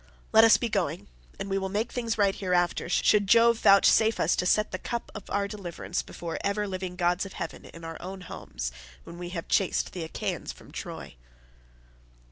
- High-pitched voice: Yes, high, 195 Hz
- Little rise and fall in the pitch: No, average, 3.1 semitones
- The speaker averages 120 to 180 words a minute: No, average, 195 wpm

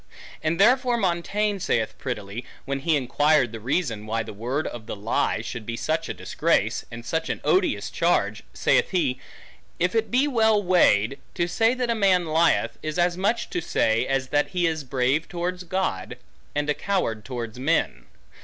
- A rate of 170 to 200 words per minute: Yes, average, 180 wpm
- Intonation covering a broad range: Yes, wide, 7.4 semitones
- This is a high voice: No, medium, 155 Hz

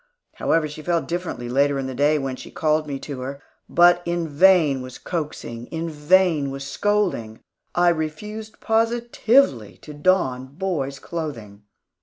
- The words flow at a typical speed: Yes, average, 150 wpm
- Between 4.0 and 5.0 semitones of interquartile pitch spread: Yes, average, 4.5 semitones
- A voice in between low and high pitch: Yes, medium, 155 Hz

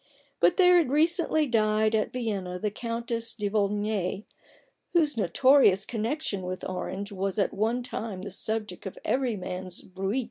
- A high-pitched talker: Yes, high, 215 Hz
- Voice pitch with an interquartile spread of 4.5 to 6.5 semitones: No, average, 4.1 semitones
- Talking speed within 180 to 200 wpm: No, average, 150 wpm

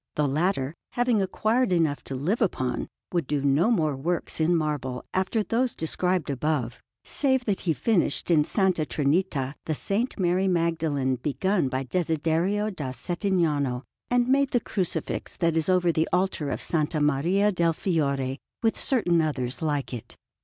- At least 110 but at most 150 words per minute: No, average, 160 wpm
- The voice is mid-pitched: Yes, medium, 165 Hz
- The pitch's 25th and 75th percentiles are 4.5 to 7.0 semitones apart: Yes, average, 5.0 semitones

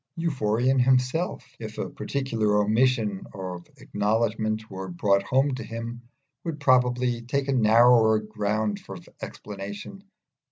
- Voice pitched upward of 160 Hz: No, low, 115 Hz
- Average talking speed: No, slow, 120 wpm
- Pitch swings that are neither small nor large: Yes, average, 3.6 semitones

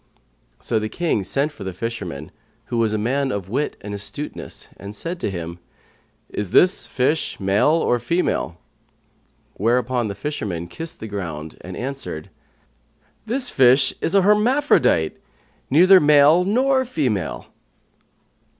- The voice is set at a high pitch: No, low, 125 Hz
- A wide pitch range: Yes, wide, 8.4 semitones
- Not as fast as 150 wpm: Yes, average, 140 wpm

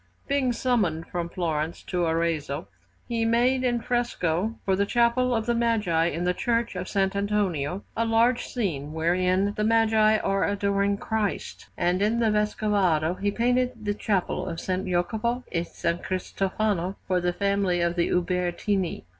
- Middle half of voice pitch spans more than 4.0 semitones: Yes, average, 4.4 semitones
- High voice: Yes, high, 200 Hz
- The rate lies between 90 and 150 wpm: No, average, 160 wpm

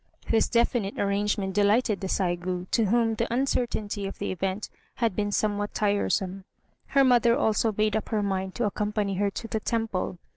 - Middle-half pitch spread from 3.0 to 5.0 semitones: No, narrow, 2.6 semitones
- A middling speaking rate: Yes, average, 175 wpm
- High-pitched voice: Yes, high, 210 Hz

